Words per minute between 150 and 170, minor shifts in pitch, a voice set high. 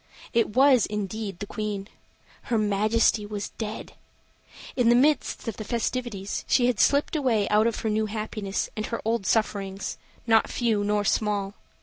Yes: average, 160 wpm; narrow, 2.2 semitones; high, 215 Hz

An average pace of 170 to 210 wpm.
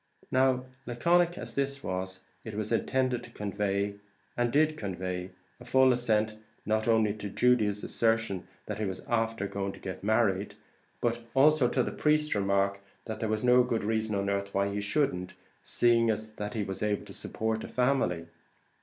Yes: average, 175 wpm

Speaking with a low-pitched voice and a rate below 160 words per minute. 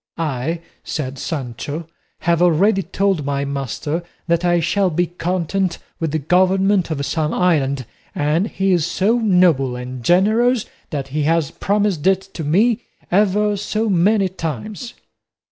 No: medium, 175 Hz; average, 145 wpm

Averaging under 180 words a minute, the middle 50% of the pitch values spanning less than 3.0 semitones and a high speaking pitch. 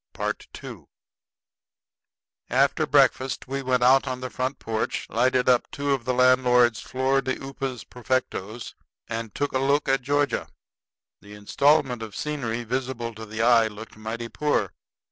No: average, 145 wpm; narrow, 2.6 semitones; low, 125 Hz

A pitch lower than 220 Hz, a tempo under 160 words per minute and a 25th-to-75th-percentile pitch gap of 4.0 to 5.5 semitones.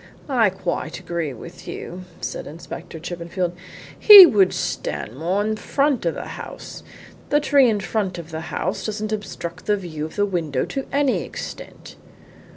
No: medium, 185 Hz; average, 165 wpm; average, 4.3 semitones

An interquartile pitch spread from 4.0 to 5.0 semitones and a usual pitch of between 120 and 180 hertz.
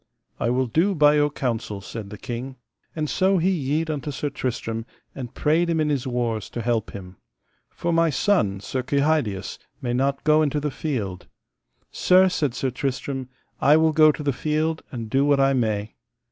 Yes: average, 4.5 semitones; medium, 140 Hz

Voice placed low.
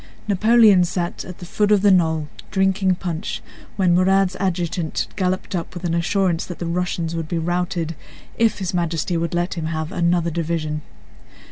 No: medium, 175 Hz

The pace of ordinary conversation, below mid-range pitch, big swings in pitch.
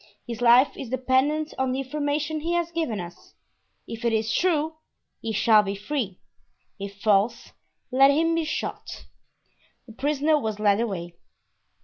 No: average, 150 wpm; very high, 255 Hz; wide, 5.7 semitones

